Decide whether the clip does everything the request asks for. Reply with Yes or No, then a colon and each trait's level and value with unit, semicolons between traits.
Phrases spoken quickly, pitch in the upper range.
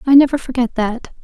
No: average, 195 wpm; very high, 255 Hz